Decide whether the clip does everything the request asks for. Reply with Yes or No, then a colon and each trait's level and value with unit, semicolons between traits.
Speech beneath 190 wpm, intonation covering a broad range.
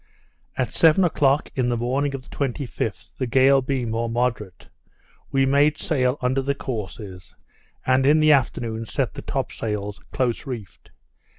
No: average, 160 wpm; average, 3.2 semitones